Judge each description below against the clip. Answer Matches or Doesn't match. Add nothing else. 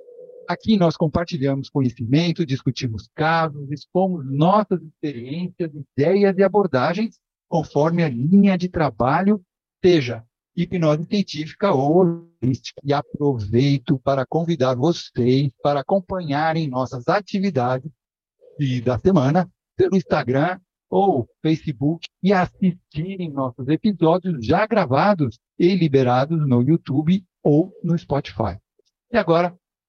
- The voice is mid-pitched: Matches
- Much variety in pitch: Doesn't match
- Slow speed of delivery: Matches